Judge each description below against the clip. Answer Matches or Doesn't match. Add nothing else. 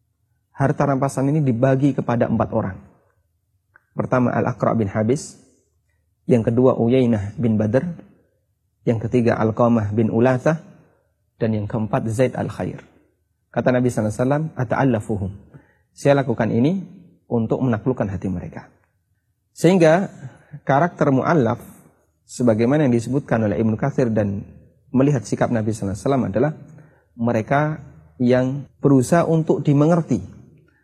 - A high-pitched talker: Doesn't match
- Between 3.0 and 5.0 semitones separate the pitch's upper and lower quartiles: Matches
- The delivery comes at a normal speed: Matches